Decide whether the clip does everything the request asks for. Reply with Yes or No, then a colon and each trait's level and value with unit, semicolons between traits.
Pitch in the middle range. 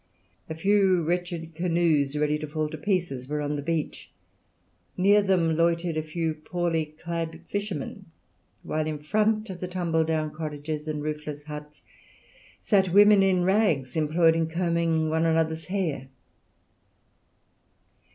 Yes: medium, 165 Hz